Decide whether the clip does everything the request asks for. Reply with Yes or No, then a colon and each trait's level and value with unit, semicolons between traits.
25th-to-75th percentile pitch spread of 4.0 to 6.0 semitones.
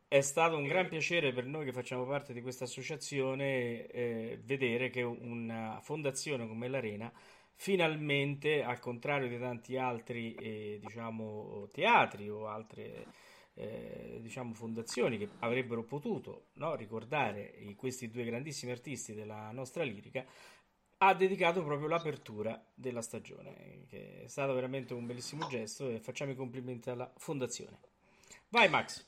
No: average, 3.2 semitones